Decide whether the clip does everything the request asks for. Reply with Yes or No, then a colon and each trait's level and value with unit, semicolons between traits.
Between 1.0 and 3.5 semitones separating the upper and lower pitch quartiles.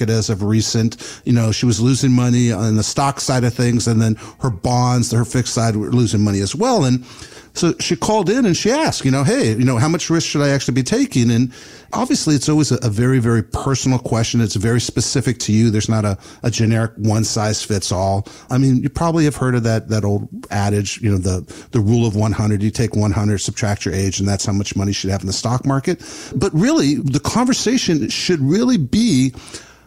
No: average, 4.1 semitones